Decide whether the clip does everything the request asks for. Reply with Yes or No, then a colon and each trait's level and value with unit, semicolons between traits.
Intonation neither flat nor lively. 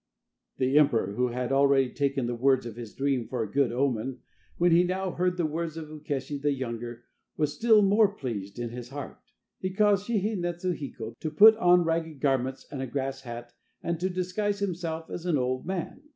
No: wide, 5.8 semitones